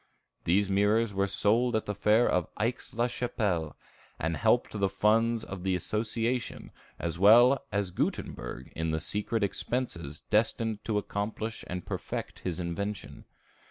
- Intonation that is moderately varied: Yes, average, 3.6 semitones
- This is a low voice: Yes, low, 105 Hz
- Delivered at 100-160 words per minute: Yes, average, 145 wpm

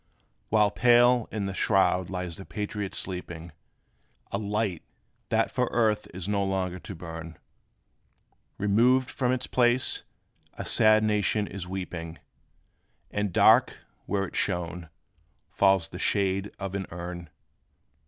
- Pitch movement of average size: Yes, average, 3.1 semitones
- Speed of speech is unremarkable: No, slow, 130 wpm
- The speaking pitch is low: Yes, low, 100 Hz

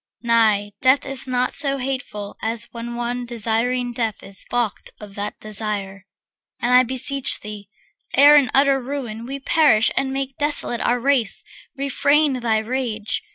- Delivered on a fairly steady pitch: No, average, 3.7 semitones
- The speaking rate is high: No, average, 155 wpm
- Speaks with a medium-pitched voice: No, high, 245 Hz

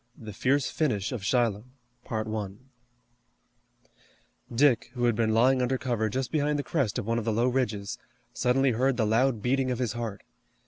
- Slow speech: No, average, 170 wpm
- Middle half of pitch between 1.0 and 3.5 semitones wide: Yes, average, 2.9 semitones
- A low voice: Yes, low, 120 Hz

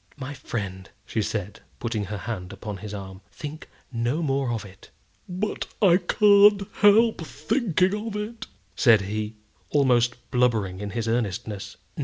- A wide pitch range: Yes, wide, 8.8 semitones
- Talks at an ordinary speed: Yes, average, 145 wpm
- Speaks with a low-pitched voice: Yes, low, 120 Hz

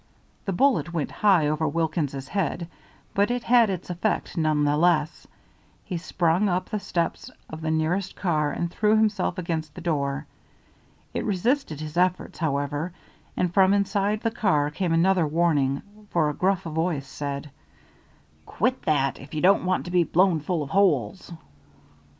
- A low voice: No, medium, 170 Hz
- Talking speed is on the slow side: No, average, 160 wpm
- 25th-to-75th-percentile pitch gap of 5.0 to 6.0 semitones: No, average, 4.1 semitones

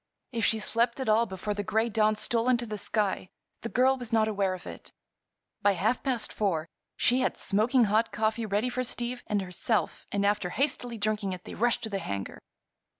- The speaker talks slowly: No, fast, 205 wpm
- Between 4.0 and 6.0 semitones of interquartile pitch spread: No, average, 2.7 semitones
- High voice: Yes, high, 220 Hz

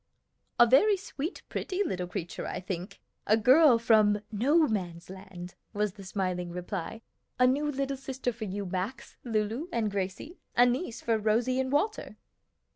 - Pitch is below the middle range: No, high, 225 Hz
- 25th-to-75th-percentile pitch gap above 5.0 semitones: Yes, wide, 5.5 semitones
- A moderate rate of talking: Yes, average, 165 wpm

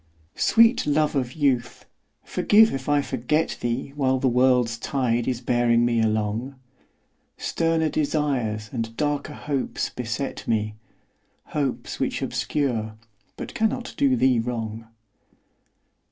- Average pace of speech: No, slow, 120 wpm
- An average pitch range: Yes, average, 4.0 semitones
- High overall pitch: No, low, 130 Hz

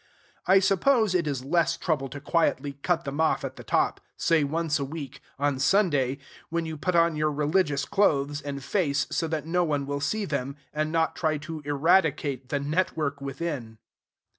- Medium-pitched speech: Yes, medium, 150 Hz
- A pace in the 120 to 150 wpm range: No, average, 185 wpm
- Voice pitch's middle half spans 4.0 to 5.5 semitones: No, average, 3.1 semitones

